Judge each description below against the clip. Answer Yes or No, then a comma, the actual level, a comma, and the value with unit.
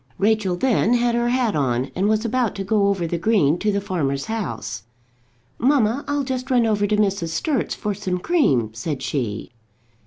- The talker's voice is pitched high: Yes, high, 205 Hz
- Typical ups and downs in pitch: No, wide, 6.5 semitones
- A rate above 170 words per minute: Yes, average, 185 wpm